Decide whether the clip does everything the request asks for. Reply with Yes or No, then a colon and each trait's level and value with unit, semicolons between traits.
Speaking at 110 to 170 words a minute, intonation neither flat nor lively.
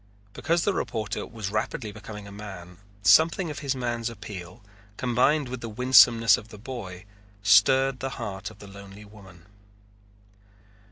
Yes: average, 150 wpm; average, 4.1 semitones